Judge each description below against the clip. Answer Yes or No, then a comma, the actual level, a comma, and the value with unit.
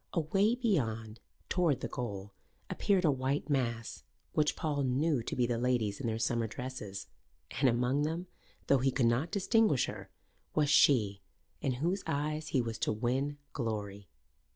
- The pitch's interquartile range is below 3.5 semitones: No, average, 4.7 semitones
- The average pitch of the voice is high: No, low, 130 Hz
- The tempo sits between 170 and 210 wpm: No, average, 160 wpm